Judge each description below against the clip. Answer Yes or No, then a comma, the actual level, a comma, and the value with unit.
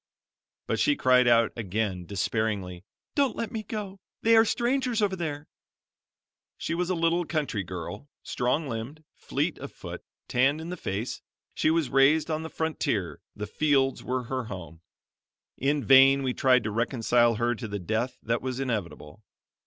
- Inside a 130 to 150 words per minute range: No, average, 165 wpm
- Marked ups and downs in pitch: Yes, wide, 6.4 semitones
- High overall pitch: No, low, 130 Hz